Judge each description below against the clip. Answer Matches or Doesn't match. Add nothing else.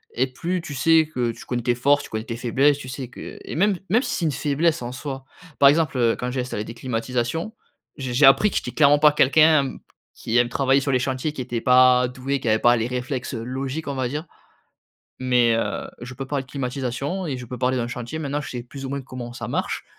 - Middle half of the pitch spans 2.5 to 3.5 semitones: Matches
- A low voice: Matches